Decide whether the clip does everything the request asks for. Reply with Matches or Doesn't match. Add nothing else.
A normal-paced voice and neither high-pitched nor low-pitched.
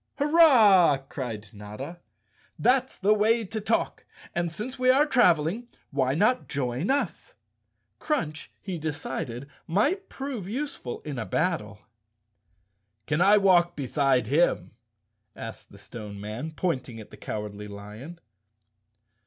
Doesn't match